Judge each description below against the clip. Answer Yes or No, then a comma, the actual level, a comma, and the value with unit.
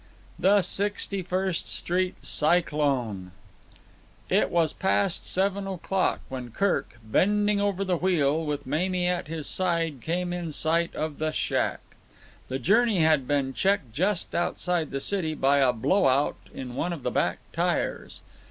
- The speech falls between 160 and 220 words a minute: No, average, 150 wpm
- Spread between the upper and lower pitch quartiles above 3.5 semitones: Yes, average, 4.7 semitones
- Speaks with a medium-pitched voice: Yes, medium, 170 Hz